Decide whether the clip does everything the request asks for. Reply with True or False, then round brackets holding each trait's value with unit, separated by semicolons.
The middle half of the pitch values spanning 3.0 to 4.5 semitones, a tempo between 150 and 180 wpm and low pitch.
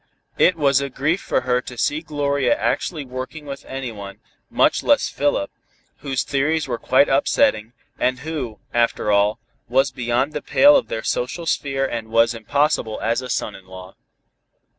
True (3.8 semitones; 165 wpm; 130 Hz)